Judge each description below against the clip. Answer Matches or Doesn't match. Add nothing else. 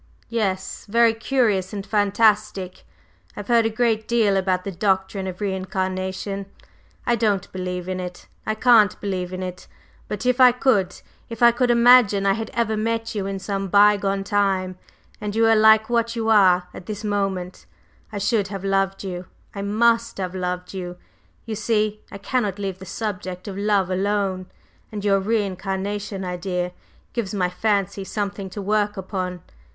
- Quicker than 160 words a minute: Matches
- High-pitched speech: Matches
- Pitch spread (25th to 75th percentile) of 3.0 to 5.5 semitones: Doesn't match